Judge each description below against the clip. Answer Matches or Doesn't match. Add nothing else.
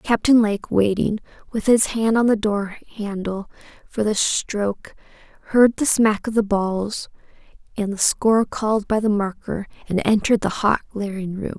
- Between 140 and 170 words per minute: Matches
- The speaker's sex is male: Doesn't match